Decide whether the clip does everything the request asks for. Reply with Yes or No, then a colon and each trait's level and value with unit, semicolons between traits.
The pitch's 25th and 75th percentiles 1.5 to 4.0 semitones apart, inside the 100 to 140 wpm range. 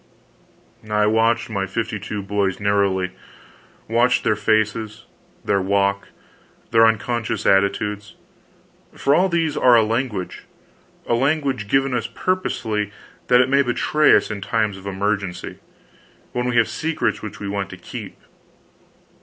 Yes: average, 3.5 semitones; slow, 135 wpm